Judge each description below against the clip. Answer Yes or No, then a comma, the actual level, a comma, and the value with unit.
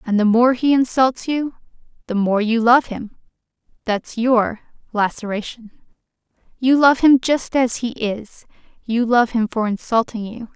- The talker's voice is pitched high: Yes, high, 235 Hz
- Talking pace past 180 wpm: No, average, 150 wpm